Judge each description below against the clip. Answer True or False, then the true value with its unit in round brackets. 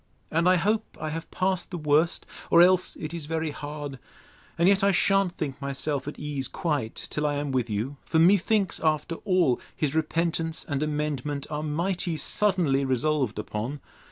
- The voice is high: False (155 Hz)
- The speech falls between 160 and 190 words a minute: True (175 wpm)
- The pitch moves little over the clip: False (3.2 semitones)